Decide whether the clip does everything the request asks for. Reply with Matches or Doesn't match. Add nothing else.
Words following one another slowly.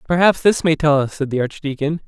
Doesn't match